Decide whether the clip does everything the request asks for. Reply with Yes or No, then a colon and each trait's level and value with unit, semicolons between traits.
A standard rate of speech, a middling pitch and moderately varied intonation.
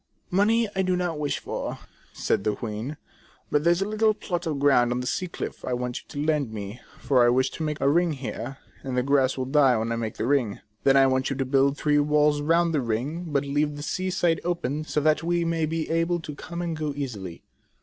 No: fast, 245 wpm; medium, 145 Hz; average, 4.2 semitones